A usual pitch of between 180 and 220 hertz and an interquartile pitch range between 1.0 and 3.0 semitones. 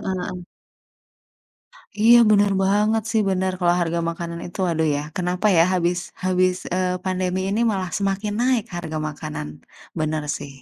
Yes: medium, 185 Hz; narrow, 2.6 semitones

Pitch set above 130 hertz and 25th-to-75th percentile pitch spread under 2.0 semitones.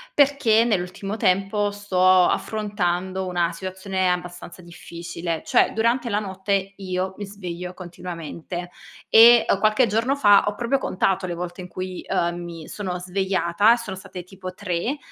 No: high, 190 Hz; narrow, 2.5 semitones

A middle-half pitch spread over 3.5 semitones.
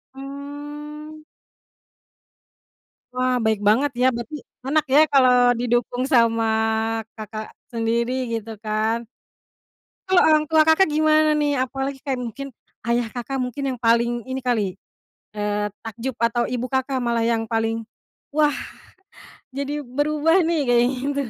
Yes: average, 3.9 semitones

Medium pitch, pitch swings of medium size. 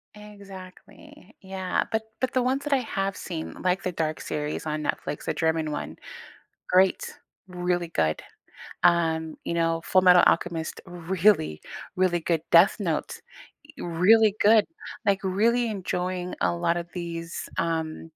Yes: medium, 180 Hz; average, 3.0 semitones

